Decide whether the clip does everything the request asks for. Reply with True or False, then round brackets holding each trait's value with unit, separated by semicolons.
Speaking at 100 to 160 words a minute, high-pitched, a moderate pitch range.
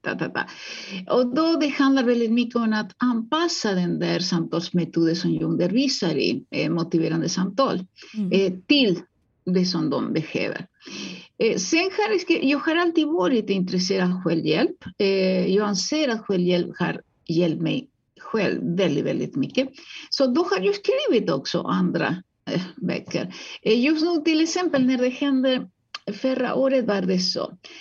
False (150 wpm; 230 Hz; 8.0 semitones)